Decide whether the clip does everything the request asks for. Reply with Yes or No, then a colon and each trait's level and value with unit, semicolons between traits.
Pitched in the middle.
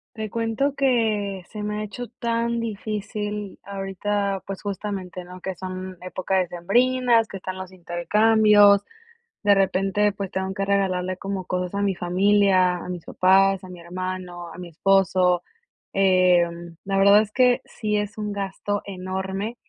No: high, 195 Hz